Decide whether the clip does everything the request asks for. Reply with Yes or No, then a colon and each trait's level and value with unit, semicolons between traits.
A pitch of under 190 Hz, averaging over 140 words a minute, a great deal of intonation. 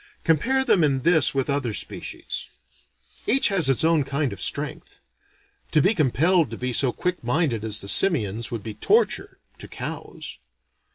Yes: medium, 140 Hz; average, 165 wpm; wide, 6.3 semitones